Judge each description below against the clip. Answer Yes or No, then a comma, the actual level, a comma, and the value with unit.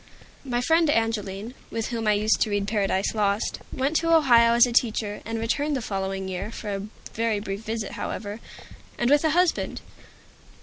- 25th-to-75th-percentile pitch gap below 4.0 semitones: Yes, average, 3.3 semitones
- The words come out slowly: No, average, 180 wpm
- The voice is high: Yes, high, 225 Hz